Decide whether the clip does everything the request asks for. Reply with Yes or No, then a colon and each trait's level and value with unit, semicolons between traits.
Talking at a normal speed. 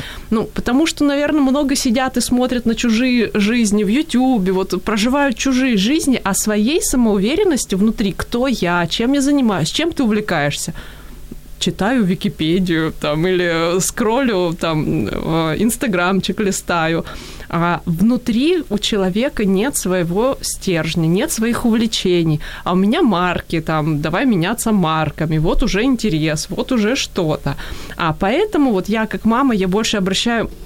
Yes: average, 135 wpm